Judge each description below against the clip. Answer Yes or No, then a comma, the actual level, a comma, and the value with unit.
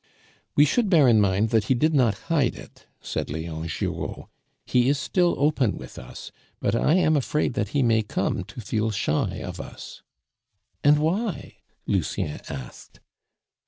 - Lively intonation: Yes, wide, 6.8 semitones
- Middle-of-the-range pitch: No, low, 125 Hz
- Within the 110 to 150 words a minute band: No, average, 160 wpm